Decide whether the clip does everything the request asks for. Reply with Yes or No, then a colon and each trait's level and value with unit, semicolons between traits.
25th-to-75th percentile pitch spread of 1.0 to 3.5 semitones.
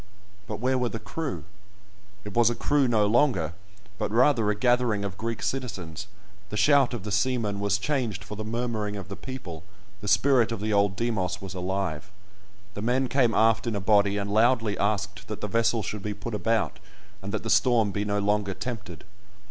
Yes: average, 3.0 semitones